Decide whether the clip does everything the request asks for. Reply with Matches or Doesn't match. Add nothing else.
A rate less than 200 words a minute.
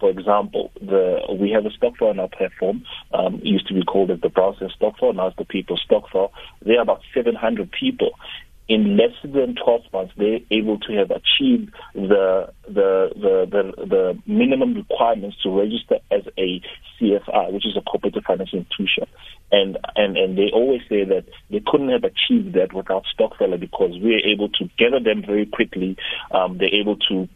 Matches